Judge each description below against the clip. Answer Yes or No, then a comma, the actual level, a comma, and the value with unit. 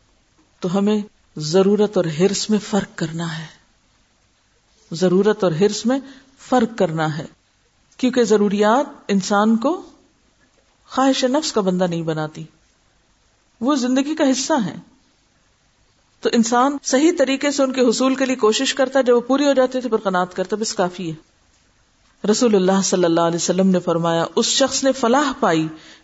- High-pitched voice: Yes, high, 210 Hz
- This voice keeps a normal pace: Yes, average, 160 wpm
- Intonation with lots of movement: Yes, wide, 7.5 semitones